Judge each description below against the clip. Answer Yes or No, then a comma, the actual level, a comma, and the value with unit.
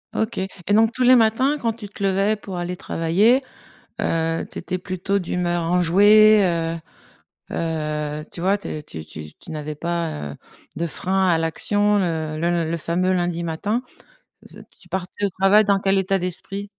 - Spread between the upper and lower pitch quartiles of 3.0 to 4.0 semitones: Yes, average, 3.6 semitones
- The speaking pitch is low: No, medium, 180 Hz